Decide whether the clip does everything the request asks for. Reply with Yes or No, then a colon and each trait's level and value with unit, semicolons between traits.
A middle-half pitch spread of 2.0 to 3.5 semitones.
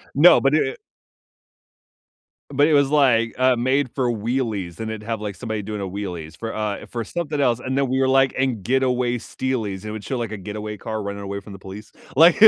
No: average, 4.1 semitones